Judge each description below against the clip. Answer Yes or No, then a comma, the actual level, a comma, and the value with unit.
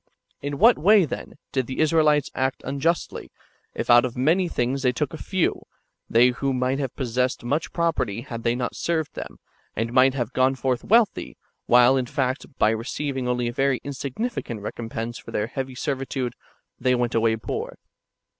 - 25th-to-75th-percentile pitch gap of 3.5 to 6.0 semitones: No, average, 2.9 semitones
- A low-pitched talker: Yes, low, 130 Hz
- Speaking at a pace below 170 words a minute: No, average, 175 wpm